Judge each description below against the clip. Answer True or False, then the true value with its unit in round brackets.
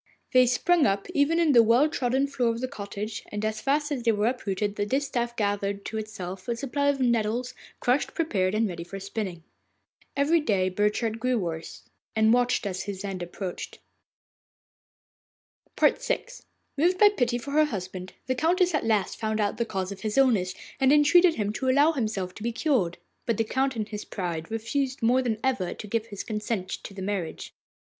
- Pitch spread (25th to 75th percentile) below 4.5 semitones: False (4.8 semitones)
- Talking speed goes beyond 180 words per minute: True (190 wpm)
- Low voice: False (225 Hz)